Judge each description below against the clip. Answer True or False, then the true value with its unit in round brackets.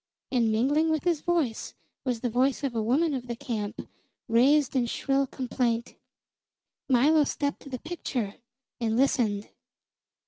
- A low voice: False (255 Hz)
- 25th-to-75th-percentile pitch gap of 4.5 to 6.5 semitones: False (3.6 semitones)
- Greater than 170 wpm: False (145 wpm)